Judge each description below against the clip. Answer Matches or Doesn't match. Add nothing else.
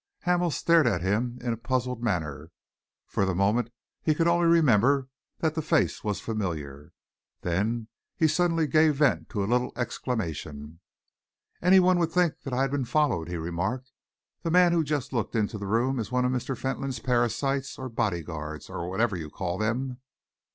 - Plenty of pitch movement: Matches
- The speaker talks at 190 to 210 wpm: Doesn't match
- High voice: Doesn't match